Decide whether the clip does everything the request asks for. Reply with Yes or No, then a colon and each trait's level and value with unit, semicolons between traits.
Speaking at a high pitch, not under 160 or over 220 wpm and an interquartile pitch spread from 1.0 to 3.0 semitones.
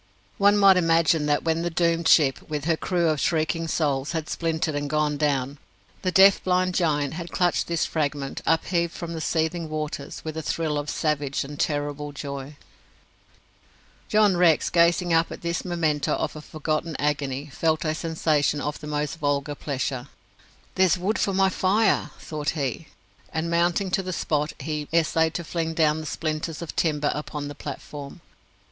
No: medium, 160 Hz; average, 175 wpm; narrow, 2.5 semitones